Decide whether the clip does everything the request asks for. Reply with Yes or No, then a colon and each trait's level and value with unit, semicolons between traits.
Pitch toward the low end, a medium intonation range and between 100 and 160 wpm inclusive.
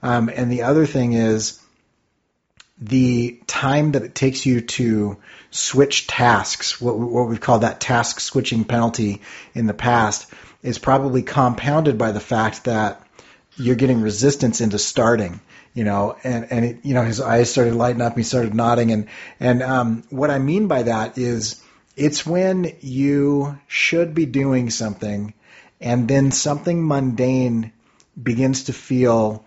Yes: low, 120 Hz; average, 3.0 semitones; average, 155 wpm